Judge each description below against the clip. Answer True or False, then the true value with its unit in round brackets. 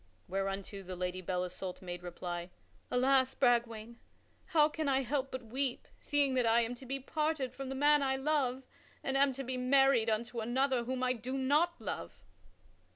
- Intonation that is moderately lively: True (3.6 semitones)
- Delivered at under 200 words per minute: True (180 wpm)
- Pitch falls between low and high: False (255 Hz)